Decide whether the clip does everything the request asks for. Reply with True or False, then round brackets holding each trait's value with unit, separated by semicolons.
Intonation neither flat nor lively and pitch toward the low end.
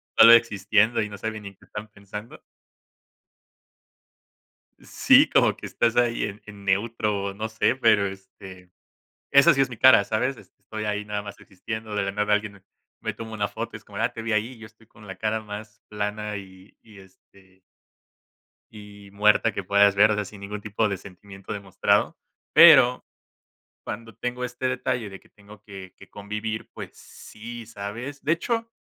False (2.0 semitones; 105 Hz)